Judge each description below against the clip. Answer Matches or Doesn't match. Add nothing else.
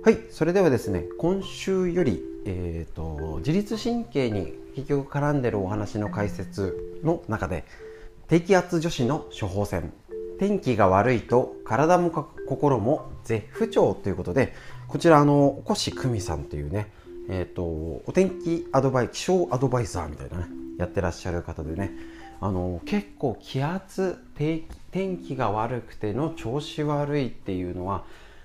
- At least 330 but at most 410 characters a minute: Doesn't match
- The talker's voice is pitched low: Matches